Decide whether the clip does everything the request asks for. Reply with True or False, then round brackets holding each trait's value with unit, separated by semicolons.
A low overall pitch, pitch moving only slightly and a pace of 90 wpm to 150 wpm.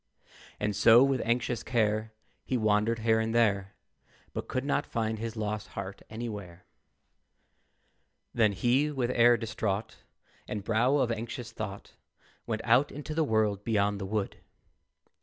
True (110 Hz; 2.3 semitones; 140 wpm)